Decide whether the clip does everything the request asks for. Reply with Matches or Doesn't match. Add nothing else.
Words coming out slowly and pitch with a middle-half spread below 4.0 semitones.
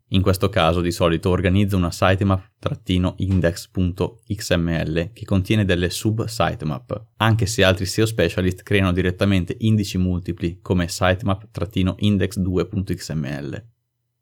Matches